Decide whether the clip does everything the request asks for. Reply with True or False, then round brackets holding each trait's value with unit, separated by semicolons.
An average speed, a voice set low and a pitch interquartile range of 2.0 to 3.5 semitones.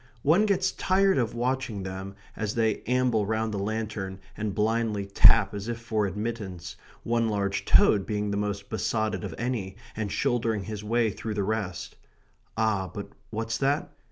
True (165 wpm; 110 Hz; 2.5 semitones)